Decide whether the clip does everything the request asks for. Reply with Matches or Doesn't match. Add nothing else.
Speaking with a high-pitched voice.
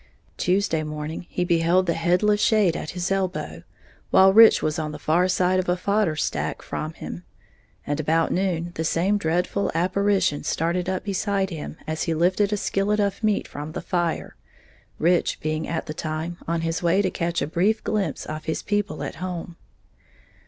Doesn't match